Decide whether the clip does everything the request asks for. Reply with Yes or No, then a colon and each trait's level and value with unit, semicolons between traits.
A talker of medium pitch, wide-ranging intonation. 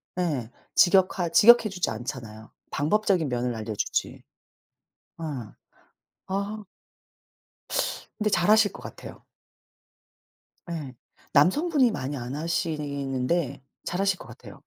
Yes: medium, 165 Hz; wide, 7.0 semitones